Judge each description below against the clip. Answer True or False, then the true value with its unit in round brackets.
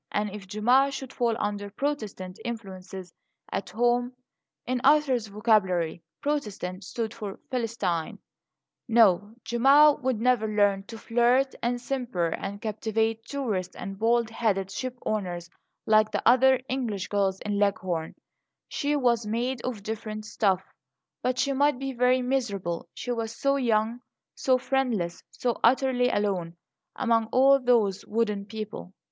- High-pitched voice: True (225 Hz)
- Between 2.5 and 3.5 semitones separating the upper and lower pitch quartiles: False (3.9 semitones)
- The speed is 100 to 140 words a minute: True (135 wpm)